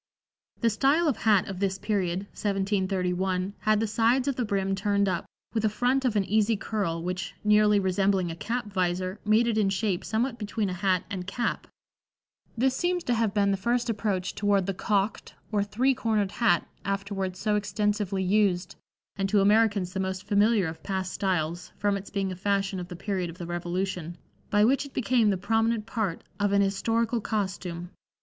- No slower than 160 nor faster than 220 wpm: Yes, average, 190 wpm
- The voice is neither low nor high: No, high, 200 Hz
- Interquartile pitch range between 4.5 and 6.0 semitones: No, narrow, 2.6 semitones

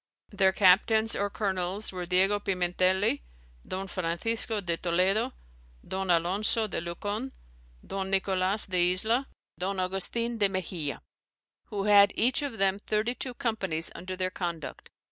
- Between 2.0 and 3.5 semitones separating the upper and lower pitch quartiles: Yes, average, 2.7 semitones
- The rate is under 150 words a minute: Yes, slow, 135 wpm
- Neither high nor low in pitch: No, high, 195 Hz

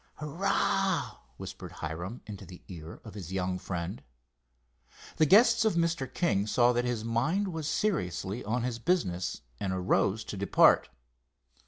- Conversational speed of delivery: Yes, average, 145 wpm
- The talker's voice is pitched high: No, low, 115 Hz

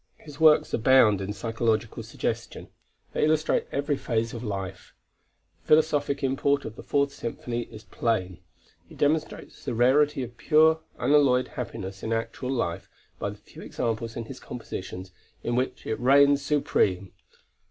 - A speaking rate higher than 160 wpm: No, average, 150 wpm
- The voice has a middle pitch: No, low, 125 Hz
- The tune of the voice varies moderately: Yes, average, 4.3 semitones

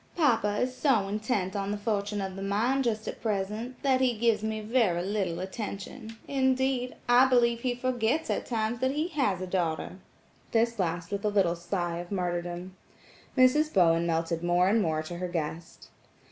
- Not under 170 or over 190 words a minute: Yes, average, 180 wpm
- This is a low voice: No, high, 210 Hz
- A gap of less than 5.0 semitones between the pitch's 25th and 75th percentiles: No, average, 5.3 semitones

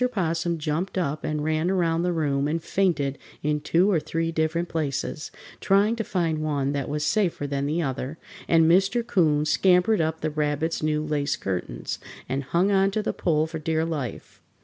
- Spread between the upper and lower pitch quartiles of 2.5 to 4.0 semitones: Yes, average, 2.9 semitones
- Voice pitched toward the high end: No, medium, 160 Hz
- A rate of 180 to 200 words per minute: Yes, average, 185 wpm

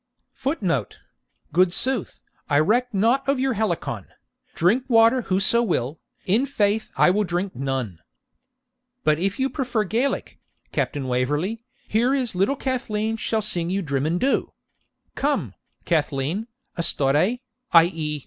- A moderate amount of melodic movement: No, wide, 7.3 semitones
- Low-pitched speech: No, high, 195 Hz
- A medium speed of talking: No, slow, 130 wpm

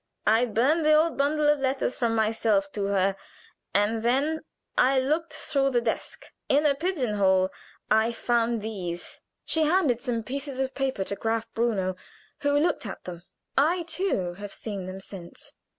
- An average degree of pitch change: No, wide, 5.7 semitones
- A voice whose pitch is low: No, high, 235 Hz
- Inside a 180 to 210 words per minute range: No, average, 165 wpm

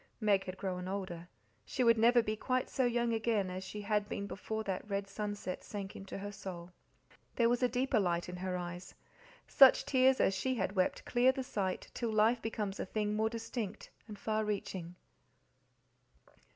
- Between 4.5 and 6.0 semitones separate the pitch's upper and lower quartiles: No, average, 3.5 semitones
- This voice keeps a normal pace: Yes, average, 185 wpm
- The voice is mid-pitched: No, high, 210 Hz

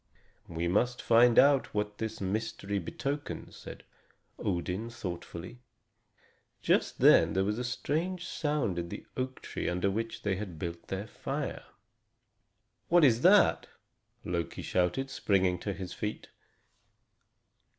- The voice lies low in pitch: Yes, low, 105 Hz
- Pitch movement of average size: No, wide, 5.7 semitones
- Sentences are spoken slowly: Yes, slow, 130 wpm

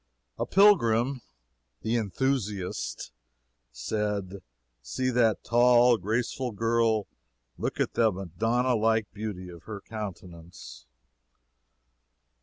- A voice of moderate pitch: No, low, 110 Hz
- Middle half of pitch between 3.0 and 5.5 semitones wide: Yes, average, 3.6 semitones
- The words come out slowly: Yes, slow, 90 wpm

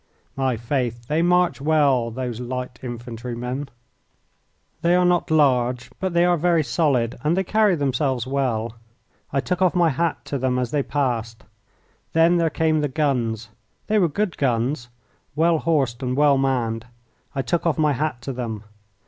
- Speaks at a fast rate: No, average, 165 wpm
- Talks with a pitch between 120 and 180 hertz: Yes, low, 135 Hz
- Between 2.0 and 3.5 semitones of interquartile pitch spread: No, average, 4.9 semitones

